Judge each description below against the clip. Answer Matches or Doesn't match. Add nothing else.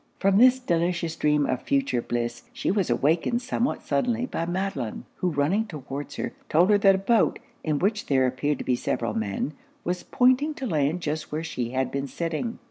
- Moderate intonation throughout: Doesn't match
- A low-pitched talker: Doesn't match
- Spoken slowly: Doesn't match